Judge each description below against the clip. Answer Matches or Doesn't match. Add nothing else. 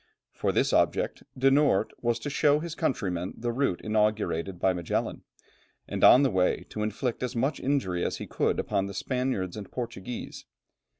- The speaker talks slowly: Doesn't match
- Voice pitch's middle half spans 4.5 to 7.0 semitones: Matches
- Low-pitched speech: Matches